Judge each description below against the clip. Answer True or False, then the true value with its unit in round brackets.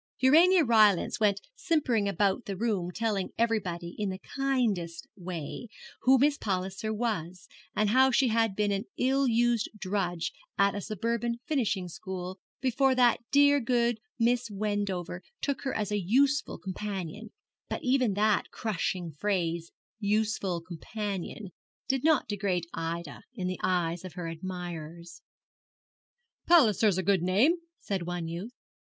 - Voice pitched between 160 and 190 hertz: False (205 Hz)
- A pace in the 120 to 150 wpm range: True (140 wpm)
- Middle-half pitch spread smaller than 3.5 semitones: False (4.6 semitones)